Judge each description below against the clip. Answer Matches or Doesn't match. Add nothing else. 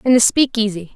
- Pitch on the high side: Matches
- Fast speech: Doesn't match